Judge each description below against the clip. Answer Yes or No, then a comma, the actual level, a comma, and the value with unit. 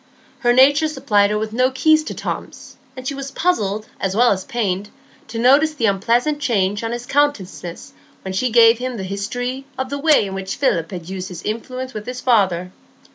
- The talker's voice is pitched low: No, high, 235 Hz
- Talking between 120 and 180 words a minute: No, average, 200 wpm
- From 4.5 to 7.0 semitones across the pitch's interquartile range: Yes, average, 4.9 semitones